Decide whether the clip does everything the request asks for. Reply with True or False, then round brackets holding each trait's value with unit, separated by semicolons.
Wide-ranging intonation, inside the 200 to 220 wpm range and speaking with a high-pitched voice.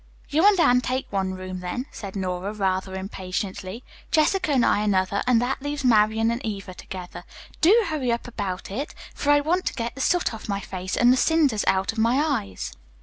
True (6.3 semitones; 205 wpm; 225 Hz)